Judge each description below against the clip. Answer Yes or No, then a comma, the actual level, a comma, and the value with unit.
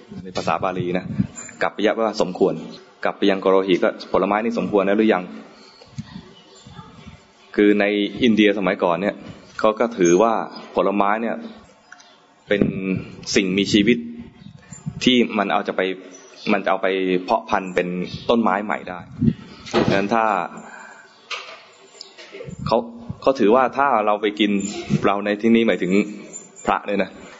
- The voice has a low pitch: Yes, low, 100 Hz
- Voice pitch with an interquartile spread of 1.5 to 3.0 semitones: Yes, average, 2.7 semitones